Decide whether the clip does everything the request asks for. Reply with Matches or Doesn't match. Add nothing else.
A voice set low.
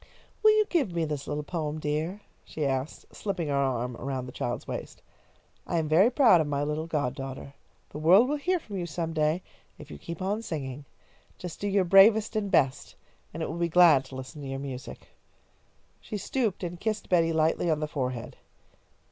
Doesn't match